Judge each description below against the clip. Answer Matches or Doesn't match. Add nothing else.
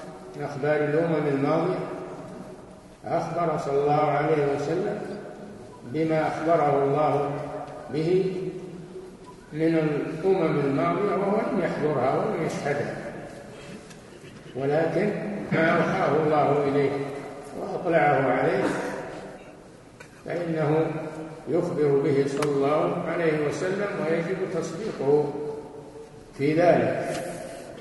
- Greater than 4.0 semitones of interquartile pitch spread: Doesn't match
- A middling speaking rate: Doesn't match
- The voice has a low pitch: Doesn't match